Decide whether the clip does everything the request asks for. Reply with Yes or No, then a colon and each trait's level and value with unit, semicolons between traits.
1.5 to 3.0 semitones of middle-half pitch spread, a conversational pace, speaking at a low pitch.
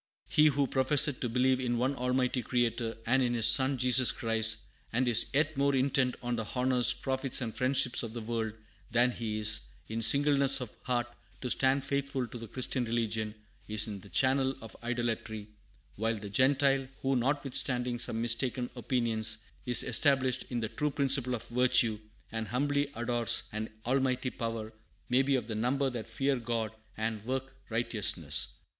Yes: average, 2.7 semitones; average, 170 wpm; low, 125 Hz